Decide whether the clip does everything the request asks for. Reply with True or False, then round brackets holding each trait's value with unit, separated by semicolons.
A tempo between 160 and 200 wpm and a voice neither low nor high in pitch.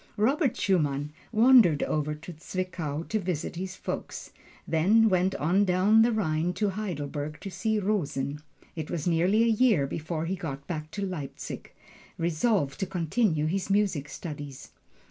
False (150 wpm; 180 Hz)